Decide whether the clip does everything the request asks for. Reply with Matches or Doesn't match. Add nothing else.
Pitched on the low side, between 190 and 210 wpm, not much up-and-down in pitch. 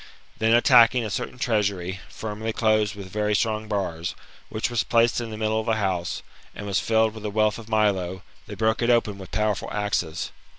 Matches